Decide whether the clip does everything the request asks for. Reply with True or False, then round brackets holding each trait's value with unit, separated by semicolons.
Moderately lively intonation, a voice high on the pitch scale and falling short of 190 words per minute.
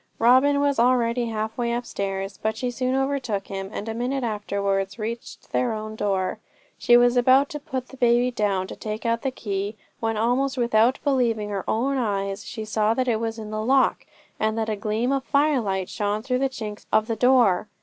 False (3.1 semitones; 230 Hz; 200 wpm)